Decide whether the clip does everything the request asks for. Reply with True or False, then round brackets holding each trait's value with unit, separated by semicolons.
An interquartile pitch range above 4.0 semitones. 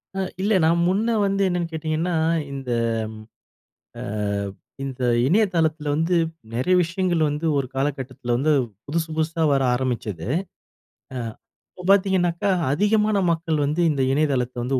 True (4.7 semitones)